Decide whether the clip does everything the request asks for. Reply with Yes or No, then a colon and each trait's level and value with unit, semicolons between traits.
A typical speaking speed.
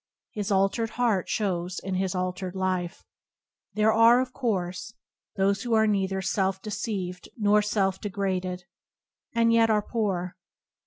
Yes: average, 145 wpm